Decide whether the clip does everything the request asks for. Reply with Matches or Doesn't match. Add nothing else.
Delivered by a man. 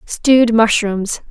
Doesn't match